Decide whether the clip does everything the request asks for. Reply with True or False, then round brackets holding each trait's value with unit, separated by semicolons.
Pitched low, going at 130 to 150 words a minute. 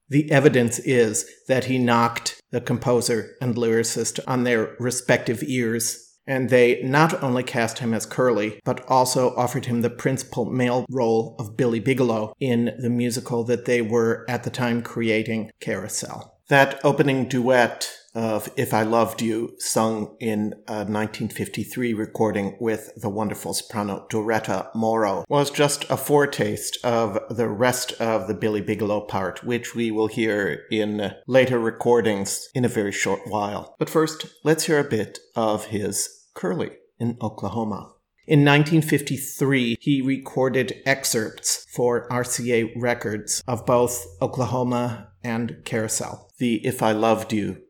True (120 Hz; 145 wpm)